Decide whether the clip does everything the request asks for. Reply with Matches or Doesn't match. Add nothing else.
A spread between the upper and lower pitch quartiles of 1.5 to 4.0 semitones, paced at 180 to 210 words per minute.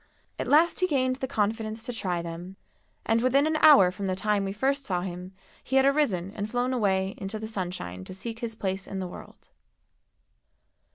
Doesn't match